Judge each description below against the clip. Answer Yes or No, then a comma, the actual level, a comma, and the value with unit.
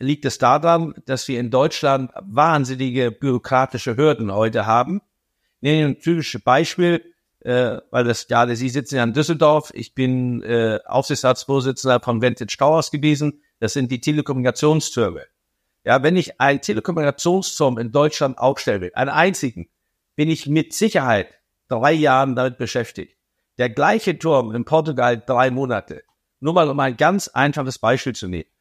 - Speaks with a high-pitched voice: No, low, 135 Hz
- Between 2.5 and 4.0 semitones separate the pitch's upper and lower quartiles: Yes, average, 3.6 semitones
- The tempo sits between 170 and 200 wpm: No, average, 155 wpm